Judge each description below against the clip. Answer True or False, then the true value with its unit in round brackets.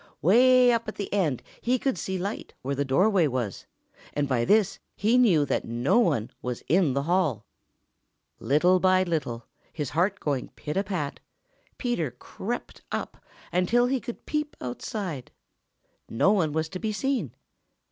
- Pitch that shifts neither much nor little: False (7.4 semitones)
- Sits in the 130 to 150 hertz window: False (180 Hz)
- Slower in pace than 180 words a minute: True (160 wpm)